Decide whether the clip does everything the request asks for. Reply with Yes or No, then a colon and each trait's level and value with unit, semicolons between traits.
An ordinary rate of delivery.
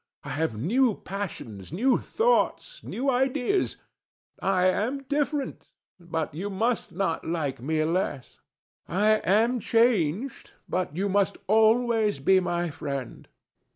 No: slow, 120 wpm